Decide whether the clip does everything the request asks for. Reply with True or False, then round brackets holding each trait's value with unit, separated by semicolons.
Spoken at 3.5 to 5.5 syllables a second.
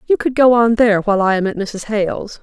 False (6.2 syllables/s)